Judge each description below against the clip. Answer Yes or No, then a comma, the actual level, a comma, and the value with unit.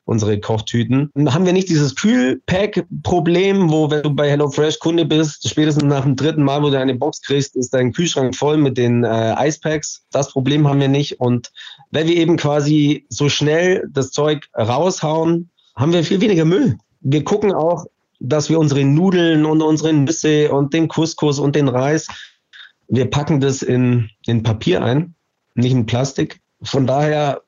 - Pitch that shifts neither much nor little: Yes, average, 3.0 semitones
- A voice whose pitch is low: No, medium, 150 Hz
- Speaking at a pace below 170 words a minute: No, average, 175 wpm